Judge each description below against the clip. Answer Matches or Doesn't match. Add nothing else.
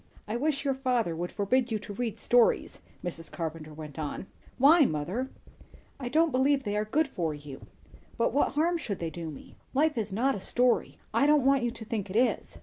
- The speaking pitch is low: Doesn't match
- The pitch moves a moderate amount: Doesn't match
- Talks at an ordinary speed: Doesn't match